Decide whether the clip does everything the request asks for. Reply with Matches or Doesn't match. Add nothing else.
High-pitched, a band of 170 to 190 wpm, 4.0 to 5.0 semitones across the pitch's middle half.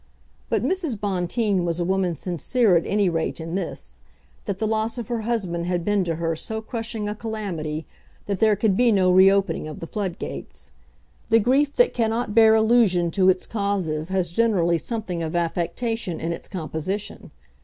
Matches